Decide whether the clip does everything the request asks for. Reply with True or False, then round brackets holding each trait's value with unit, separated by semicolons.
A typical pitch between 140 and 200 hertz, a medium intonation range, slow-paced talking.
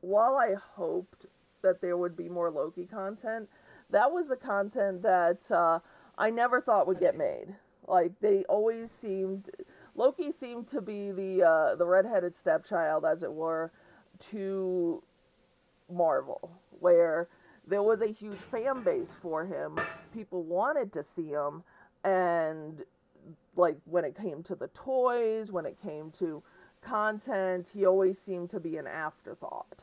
False (190 Hz; 3.7 semitones; 150 wpm)